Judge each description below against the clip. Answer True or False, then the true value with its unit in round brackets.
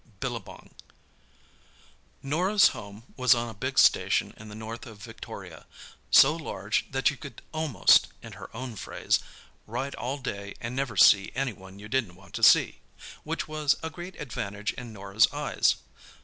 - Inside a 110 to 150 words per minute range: False (160 wpm)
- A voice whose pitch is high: False (120 Hz)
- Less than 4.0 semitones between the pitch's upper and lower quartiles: False (4.8 semitones)